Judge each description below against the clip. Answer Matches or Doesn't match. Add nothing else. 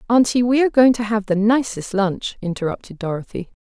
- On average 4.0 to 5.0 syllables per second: Doesn't match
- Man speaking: Doesn't match